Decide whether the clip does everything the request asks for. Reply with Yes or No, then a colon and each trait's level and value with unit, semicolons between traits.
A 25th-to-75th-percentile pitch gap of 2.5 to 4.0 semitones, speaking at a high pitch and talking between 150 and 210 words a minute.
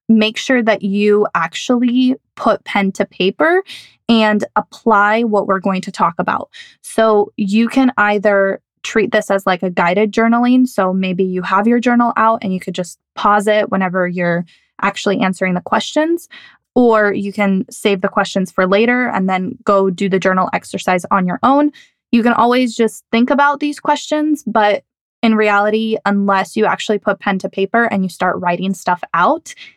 Yes: average, 3.6 semitones; high, 210 Hz; average, 180 wpm